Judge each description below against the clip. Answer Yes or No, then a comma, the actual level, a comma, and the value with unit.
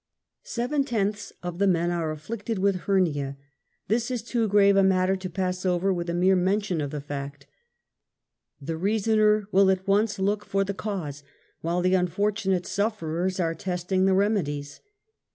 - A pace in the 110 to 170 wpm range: Yes, average, 165 wpm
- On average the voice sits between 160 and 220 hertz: Yes, high, 190 Hz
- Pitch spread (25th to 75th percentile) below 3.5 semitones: Yes, average, 2.9 semitones